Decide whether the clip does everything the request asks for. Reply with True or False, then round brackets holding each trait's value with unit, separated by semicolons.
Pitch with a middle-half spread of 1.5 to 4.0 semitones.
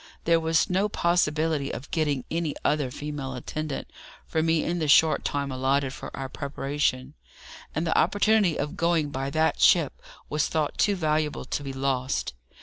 True (2.8 semitones)